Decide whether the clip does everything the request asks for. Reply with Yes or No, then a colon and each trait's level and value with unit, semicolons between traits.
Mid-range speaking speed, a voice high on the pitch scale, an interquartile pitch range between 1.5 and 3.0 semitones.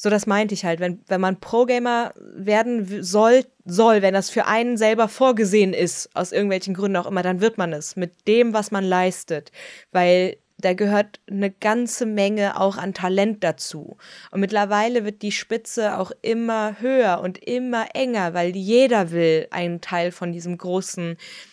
No: average, 175 wpm; high, 200 Hz; average, 3.6 semitones